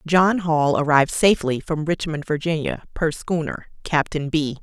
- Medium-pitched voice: Yes, medium, 155 Hz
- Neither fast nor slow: Yes, average, 145 wpm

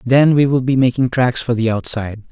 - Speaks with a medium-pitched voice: No, low, 125 Hz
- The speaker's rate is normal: No, fast, 235 wpm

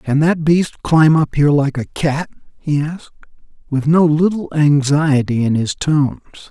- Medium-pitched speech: Yes, medium, 150 Hz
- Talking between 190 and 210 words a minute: No, average, 165 wpm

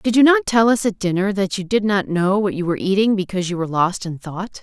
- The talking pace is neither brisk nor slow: No, fast, 285 wpm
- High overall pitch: Yes, high, 195 Hz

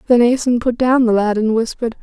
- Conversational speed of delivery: No, fast, 235 wpm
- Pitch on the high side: Yes, high, 235 Hz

